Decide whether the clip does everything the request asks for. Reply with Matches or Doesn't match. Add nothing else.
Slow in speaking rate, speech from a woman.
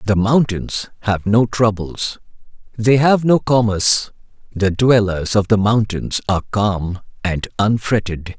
Doesn't match